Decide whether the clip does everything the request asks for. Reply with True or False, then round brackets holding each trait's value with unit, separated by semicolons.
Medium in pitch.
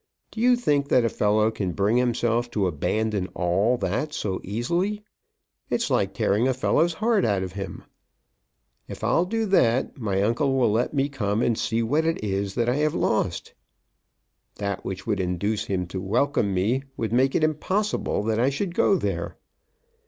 False (115 Hz)